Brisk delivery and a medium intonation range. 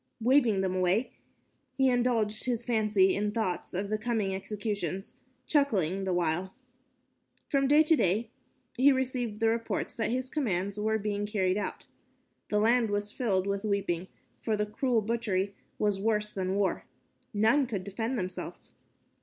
No: average, 150 wpm; average, 3.4 semitones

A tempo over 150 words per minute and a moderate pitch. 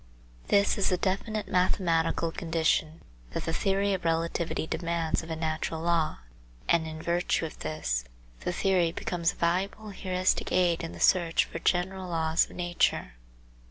Yes: average, 160 wpm; medium, 170 Hz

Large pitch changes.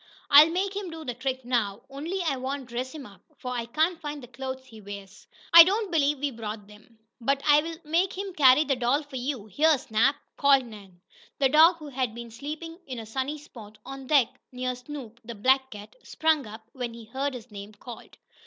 No: average, 4.4 semitones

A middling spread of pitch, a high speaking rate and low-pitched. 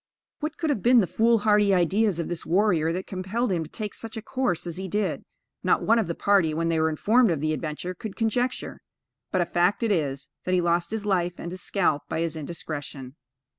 No: average, 4.6 semitones; fast, 225 wpm; medium, 185 Hz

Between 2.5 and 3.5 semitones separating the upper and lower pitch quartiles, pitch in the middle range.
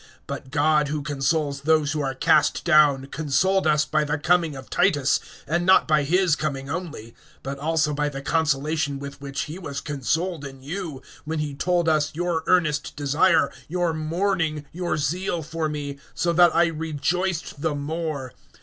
Yes: average, 2.8 semitones; medium, 155 Hz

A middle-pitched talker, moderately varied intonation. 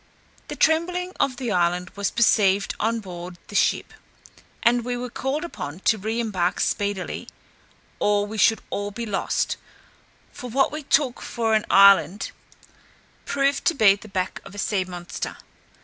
No: high, 215 Hz; average, 4.0 semitones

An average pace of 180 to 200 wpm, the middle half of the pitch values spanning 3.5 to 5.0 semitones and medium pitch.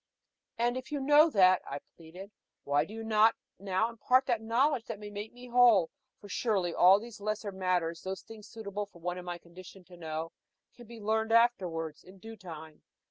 No: average, 195 wpm; average, 4.3 semitones; high, 205 Hz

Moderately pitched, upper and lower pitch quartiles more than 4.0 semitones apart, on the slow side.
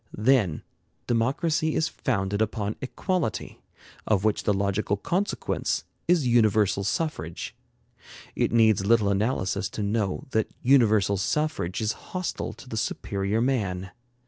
No: low, 110 Hz; average, 4.5 semitones; slow, 120 wpm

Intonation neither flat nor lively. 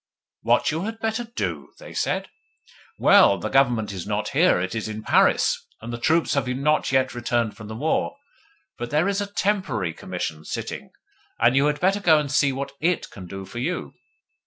No: wide, 7.2 semitones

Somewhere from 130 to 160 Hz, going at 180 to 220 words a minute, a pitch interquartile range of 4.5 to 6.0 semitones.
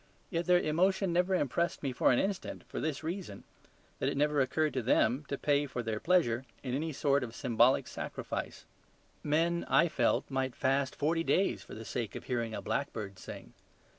Yes: medium, 140 Hz; average, 190 wpm; average, 5.2 semitones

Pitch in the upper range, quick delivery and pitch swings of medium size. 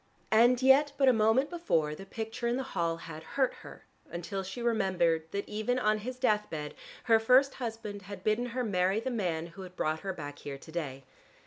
No: high, 210 Hz; fast, 210 wpm; wide, 6.2 semitones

